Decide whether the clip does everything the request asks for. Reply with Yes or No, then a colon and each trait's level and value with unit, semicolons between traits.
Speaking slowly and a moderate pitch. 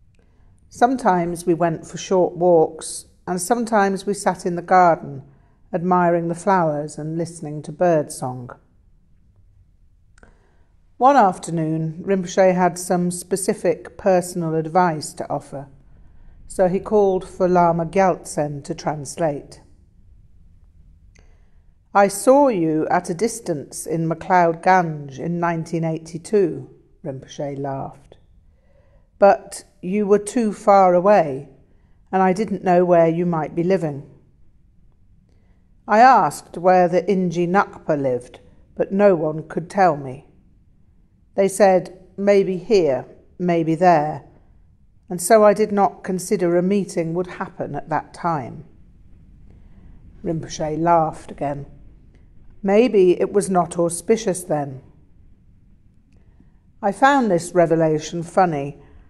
Yes: slow, 115 wpm; medium, 170 Hz